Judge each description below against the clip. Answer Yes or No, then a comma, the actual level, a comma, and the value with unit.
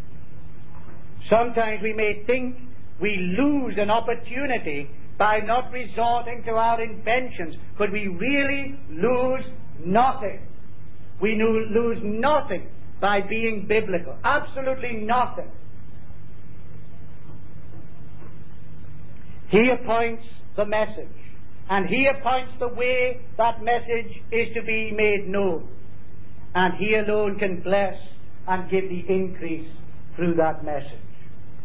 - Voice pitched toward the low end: No, high, 215 Hz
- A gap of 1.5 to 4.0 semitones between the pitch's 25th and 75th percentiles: No, average, 5.1 semitones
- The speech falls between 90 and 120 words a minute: Yes, slow, 105 wpm